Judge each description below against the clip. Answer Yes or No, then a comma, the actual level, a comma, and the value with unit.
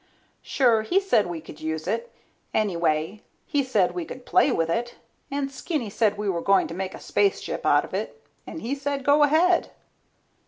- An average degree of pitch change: No, wide, 8.0 semitones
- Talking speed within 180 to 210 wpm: Yes, average, 190 wpm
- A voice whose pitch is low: No, high, 225 Hz